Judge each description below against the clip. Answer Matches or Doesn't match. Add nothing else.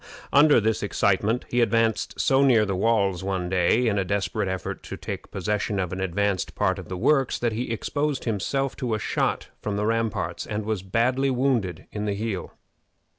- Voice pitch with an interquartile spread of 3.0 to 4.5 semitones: Matches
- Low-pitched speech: Matches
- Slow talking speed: Doesn't match